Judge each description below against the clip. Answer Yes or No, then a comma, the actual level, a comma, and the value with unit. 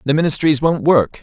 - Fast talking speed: No, average, 195 wpm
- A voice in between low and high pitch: Yes, medium, 150 Hz